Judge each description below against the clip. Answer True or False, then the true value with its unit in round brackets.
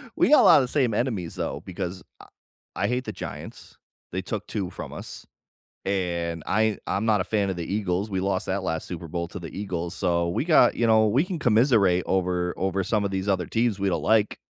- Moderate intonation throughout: True (3.6 semitones)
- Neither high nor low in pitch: False (95 Hz)